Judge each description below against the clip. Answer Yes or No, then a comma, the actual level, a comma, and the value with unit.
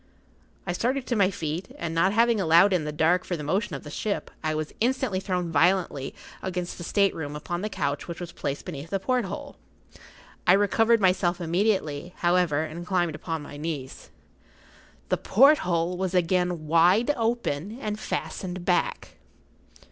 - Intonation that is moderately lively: Yes, average, 3.6 semitones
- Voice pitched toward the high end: No, medium, 180 Hz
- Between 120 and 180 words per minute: Yes, average, 165 wpm